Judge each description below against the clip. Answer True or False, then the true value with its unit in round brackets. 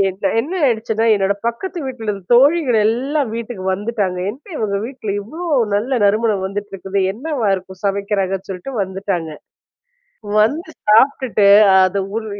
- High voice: True (215 Hz)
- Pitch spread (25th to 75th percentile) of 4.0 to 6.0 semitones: True (4.4 semitones)